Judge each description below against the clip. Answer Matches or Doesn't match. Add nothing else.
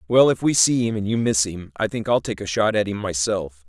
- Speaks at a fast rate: Matches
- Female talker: Doesn't match